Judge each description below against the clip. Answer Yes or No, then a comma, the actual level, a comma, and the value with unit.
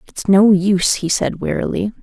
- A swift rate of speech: No, average, 180 wpm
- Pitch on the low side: No, high, 195 Hz